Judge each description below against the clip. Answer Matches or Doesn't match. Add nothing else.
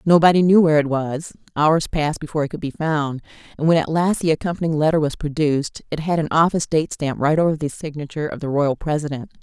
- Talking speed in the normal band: Doesn't match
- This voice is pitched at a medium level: Matches